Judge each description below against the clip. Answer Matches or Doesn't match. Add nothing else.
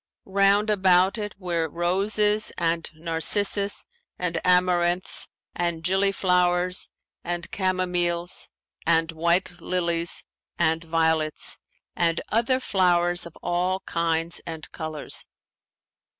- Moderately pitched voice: Matches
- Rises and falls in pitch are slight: Matches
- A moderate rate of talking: Doesn't match